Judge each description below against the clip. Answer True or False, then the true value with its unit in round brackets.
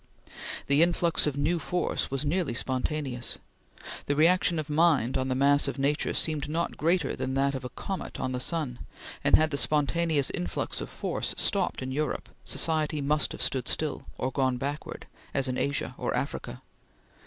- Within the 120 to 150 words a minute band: False (175 wpm)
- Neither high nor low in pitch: True (145 Hz)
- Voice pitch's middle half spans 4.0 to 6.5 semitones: False (3.1 semitones)